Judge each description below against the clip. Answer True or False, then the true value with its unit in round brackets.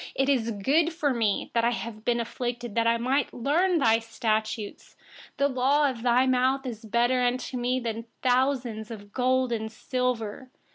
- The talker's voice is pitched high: True (245 Hz)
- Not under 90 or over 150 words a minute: False (185 wpm)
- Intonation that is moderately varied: False (2.3 semitones)